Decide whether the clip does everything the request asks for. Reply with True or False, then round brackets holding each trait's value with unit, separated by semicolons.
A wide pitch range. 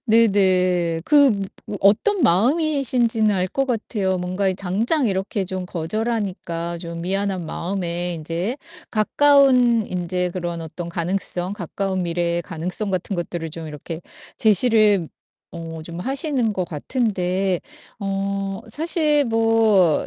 False (4.5 semitones)